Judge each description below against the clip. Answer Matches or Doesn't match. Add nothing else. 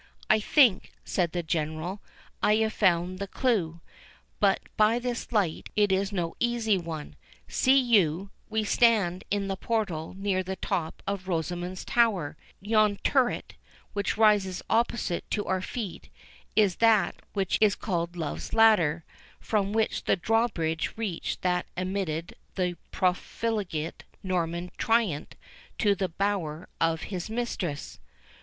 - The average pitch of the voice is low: Doesn't match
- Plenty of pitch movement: Doesn't match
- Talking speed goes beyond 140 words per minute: Doesn't match